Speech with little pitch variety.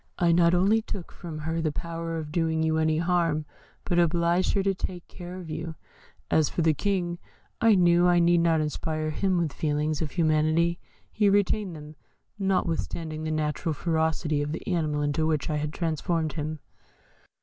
Yes: narrow, 2.0 semitones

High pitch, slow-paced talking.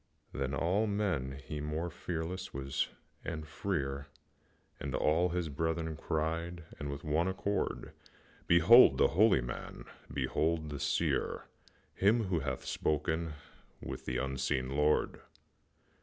No: very low, 80 Hz; slow, 120 wpm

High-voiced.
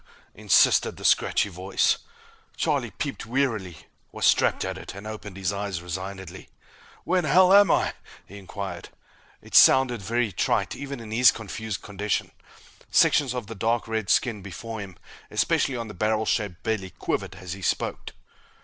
No: low, 110 Hz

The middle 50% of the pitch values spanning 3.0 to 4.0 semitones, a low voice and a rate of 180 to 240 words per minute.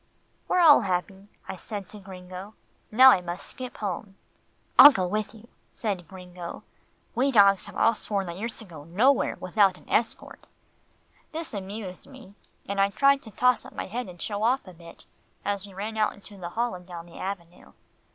No: average, 3.7 semitones; high, 200 Hz; average, 190 wpm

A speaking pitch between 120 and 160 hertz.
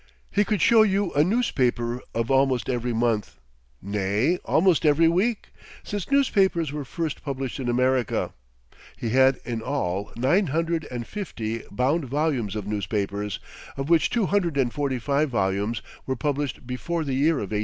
Yes: low, 135 Hz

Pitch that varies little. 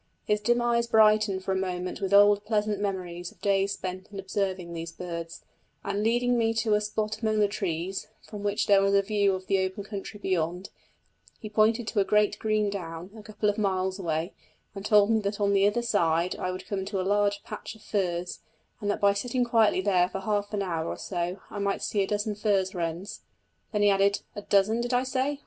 Yes: narrow, 2.1 semitones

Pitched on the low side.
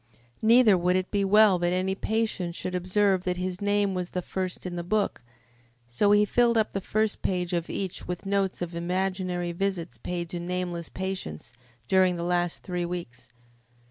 No: medium, 185 Hz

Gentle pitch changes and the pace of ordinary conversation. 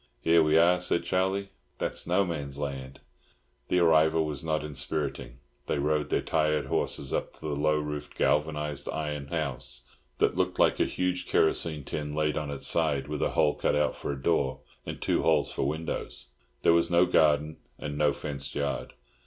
Yes: narrow, 2.2 semitones; average, 180 wpm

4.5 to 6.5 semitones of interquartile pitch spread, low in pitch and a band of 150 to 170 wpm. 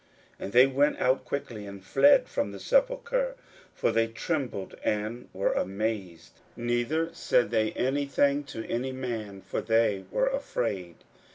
Yes: average, 5.2 semitones; low, 120 Hz; average, 155 wpm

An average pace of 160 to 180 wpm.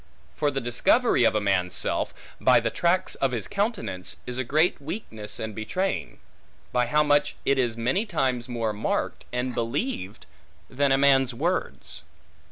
Yes: average, 170 wpm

